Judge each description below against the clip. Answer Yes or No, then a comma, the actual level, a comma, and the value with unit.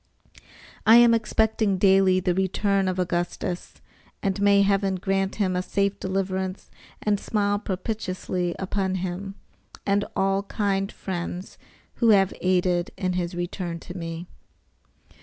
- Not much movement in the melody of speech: Yes, narrow, 1.7 semitones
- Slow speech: Yes, slow, 130 wpm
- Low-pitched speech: No, high, 190 Hz